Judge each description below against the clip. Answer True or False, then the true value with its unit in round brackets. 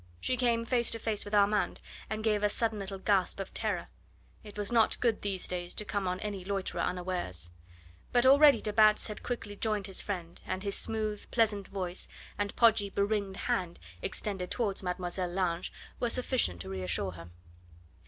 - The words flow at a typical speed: True (180 wpm)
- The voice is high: True (200 Hz)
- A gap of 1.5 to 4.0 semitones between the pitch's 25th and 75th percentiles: True (3.0 semitones)